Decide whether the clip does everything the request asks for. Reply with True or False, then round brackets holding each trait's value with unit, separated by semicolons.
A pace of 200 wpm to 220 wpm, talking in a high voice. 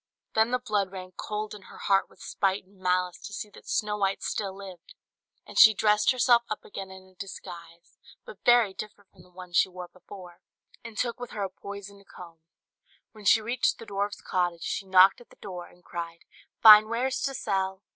True (205 wpm; 195 Hz)